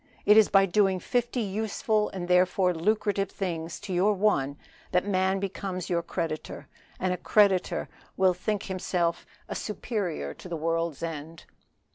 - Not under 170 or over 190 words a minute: No, average, 145 wpm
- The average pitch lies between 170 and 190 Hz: Yes, medium, 185 Hz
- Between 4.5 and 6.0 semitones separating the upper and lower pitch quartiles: No, average, 3.2 semitones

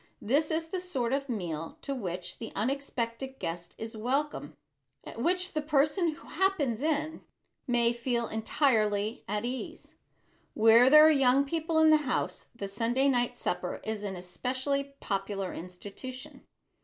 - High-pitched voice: Yes, very high, 250 Hz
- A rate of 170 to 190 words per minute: No, average, 150 wpm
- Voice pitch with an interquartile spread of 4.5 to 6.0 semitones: Yes, average, 5.3 semitones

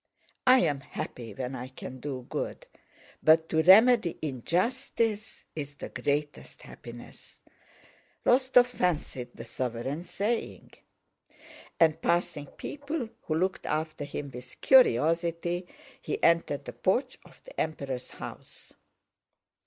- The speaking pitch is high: No, medium, 160 Hz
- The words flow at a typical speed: No, slow, 115 wpm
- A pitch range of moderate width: No, wide, 7.2 semitones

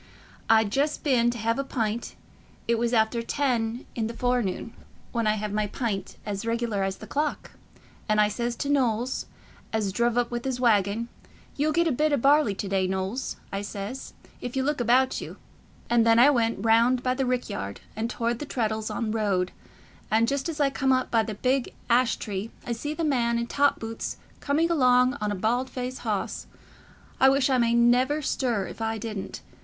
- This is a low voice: No, high, 235 Hz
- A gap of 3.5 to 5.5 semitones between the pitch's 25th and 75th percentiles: No, average, 3.0 semitones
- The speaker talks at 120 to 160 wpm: No, average, 200 wpm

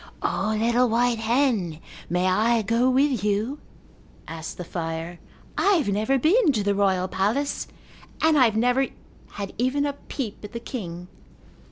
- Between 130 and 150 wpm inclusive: No, average, 160 wpm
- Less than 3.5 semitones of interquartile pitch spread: No, average, 5.0 semitones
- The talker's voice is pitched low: No, high, 225 Hz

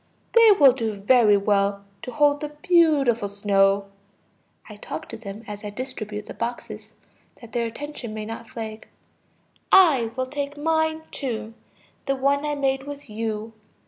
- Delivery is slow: No, average, 155 wpm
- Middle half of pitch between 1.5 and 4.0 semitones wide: No, average, 5.3 semitones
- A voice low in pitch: No, high, 235 Hz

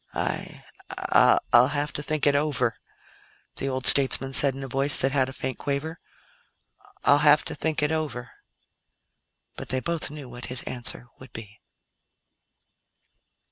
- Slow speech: No, average, 150 wpm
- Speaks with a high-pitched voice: No, low, 135 Hz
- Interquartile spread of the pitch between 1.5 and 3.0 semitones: Yes, narrow, 2.4 semitones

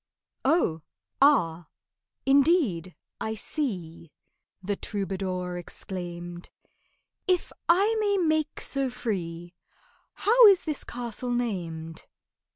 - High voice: Yes, high, 210 Hz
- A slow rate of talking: Yes, slow, 80 wpm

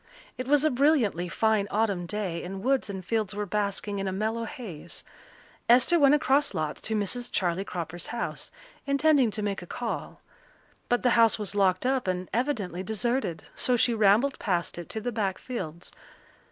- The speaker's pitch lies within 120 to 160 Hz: No, high, 215 Hz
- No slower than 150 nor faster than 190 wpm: Yes, average, 180 wpm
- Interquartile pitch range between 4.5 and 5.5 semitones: Yes, average, 4.8 semitones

